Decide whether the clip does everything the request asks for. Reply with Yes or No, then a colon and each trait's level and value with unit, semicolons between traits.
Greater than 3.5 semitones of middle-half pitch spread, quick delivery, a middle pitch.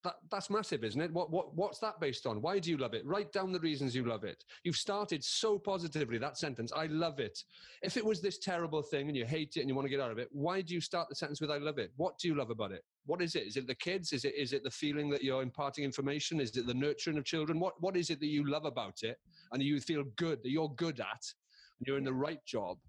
Yes: average, 4.0 semitones; fast, 295 wpm; medium, 155 Hz